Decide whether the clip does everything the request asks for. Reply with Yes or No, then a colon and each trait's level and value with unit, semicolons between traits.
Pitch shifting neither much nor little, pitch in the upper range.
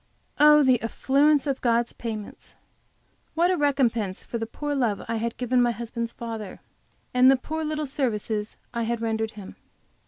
Yes: average, 3.7 semitones; high, 235 Hz